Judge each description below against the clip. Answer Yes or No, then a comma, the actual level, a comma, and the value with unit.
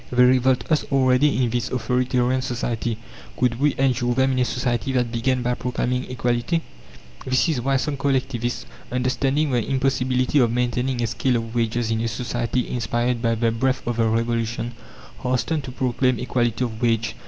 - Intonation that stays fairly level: Yes, narrow, 1.6 semitones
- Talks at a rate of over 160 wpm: Yes, average, 175 wpm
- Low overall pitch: Yes, low, 125 Hz